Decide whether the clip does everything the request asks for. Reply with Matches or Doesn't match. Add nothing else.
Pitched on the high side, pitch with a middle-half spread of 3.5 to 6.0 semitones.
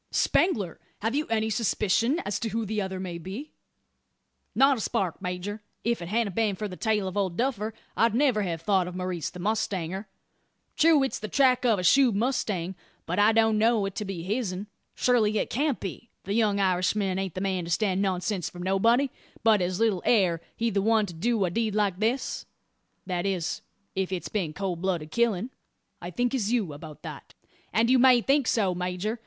Matches